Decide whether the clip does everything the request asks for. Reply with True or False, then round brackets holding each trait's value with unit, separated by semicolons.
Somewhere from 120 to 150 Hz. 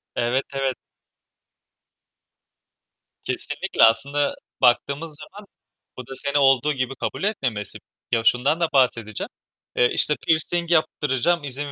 True (140 Hz)